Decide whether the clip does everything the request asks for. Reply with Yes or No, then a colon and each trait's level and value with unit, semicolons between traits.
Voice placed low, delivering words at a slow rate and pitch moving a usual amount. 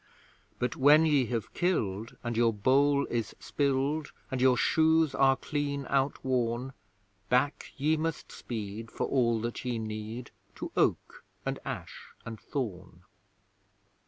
Yes: low, 130 Hz; slow, 130 wpm; average, 3.8 semitones